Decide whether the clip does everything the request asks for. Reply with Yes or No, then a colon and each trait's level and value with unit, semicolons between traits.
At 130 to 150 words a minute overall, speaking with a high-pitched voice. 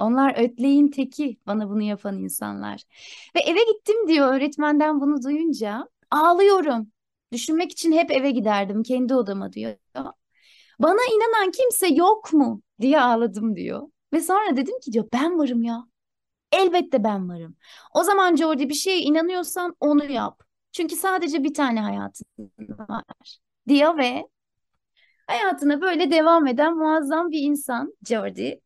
Yes: fast, 140 wpm; very high, 290 Hz